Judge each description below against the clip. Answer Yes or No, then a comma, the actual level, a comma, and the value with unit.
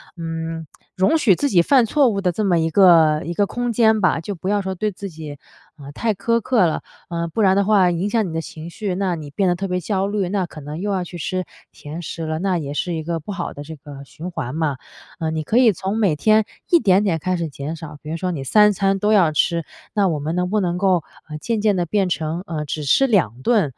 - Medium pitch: Yes, medium, 180 Hz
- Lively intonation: No, average, 4.1 semitones